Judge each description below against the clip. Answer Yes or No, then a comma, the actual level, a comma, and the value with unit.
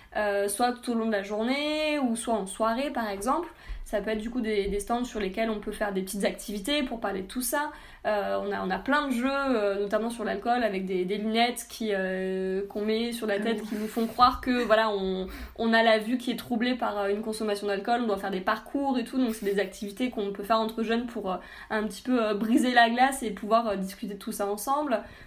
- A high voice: Yes, high, 220 Hz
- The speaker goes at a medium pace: No, fast, 260 wpm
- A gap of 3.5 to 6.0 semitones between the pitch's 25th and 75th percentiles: No, average, 3.0 semitones